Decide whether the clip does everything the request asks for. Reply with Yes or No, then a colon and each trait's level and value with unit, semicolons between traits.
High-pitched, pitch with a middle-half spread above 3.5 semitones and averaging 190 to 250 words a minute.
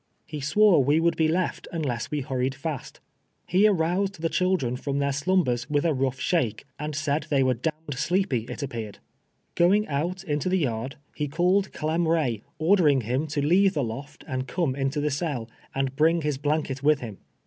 No: medium, 150 Hz; average, 4.0 semitones; average, 195 wpm